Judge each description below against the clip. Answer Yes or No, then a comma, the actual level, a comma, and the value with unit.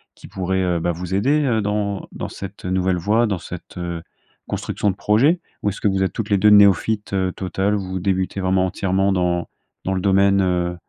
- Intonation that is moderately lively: No, narrow, 2.0 semitones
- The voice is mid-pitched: No, very low, 95 Hz